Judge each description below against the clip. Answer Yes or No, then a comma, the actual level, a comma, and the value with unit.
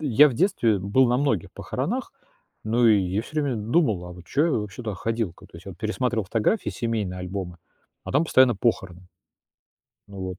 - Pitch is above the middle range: No, low, 110 Hz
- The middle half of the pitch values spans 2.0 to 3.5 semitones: No, average, 4.9 semitones